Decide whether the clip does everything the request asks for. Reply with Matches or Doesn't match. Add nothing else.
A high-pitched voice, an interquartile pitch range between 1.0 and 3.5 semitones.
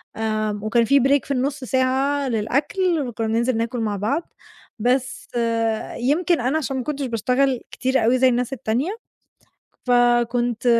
Matches